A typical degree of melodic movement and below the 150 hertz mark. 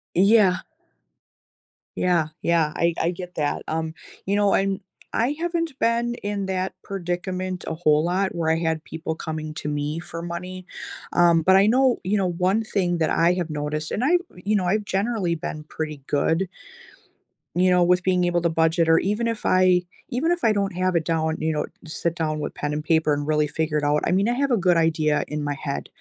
No: average, 3.5 semitones; medium, 175 Hz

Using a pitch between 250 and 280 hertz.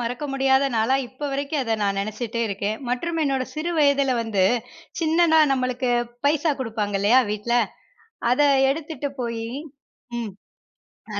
Yes: very high, 255 Hz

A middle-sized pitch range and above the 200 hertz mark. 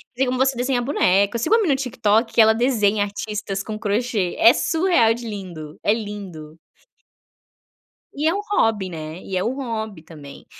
Yes: average, 4.4 semitones; high, 220 Hz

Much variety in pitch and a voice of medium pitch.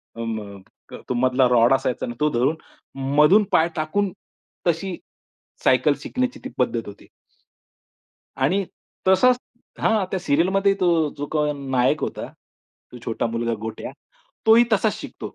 Yes: wide, 7.9 semitones; medium, 150 Hz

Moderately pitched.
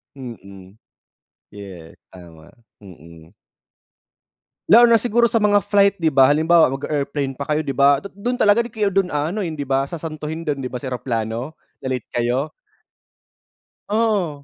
Yes: medium, 145 Hz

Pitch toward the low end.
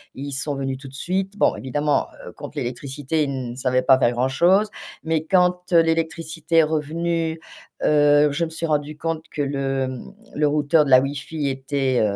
No: medium, 145 Hz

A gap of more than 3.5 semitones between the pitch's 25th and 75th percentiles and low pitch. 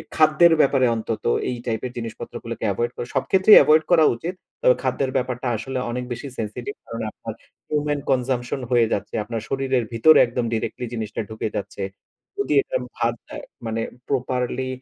Yes: average, 4.1 semitones; low, 125 Hz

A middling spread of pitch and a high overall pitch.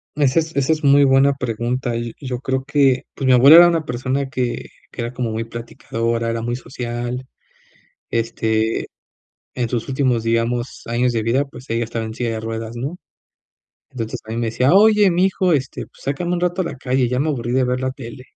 No: average, 3.1 semitones; low, 125 Hz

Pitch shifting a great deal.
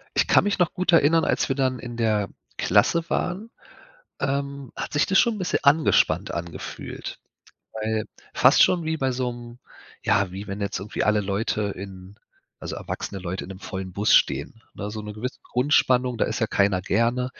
Yes: wide, 5.8 semitones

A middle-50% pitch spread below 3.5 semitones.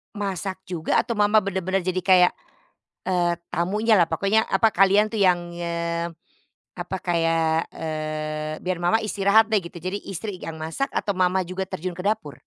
Yes: average, 2.9 semitones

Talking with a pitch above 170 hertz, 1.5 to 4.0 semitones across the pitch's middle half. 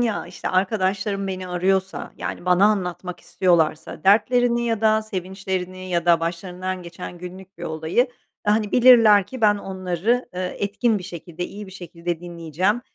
Yes: medium, 185 Hz; average, 2.8 semitones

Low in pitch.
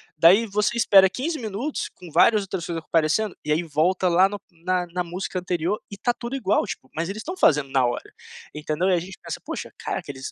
No: medium, 185 Hz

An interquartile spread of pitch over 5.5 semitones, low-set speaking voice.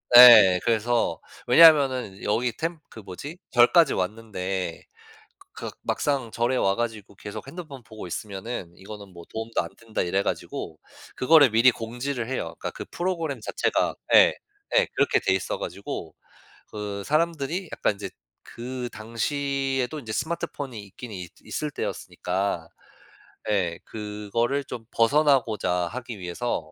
No: average, 5.1 semitones; low, 115 Hz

